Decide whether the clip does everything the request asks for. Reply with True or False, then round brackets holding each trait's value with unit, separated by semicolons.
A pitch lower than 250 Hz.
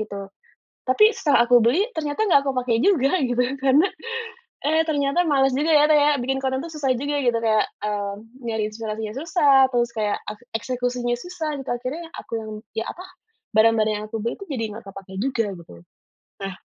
False (255 Hz)